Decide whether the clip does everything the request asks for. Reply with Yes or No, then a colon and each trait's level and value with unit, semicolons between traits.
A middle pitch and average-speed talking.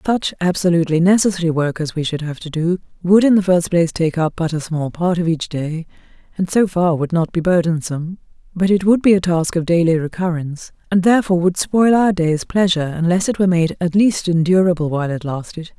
No: medium, 175 Hz; fast, 215 wpm